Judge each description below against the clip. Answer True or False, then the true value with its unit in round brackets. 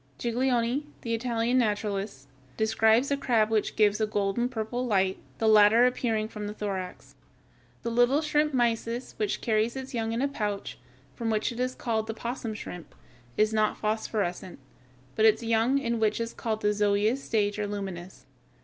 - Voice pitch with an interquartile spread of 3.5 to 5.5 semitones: False (2.4 semitones)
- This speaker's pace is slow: False (170 wpm)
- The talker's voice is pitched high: True (220 Hz)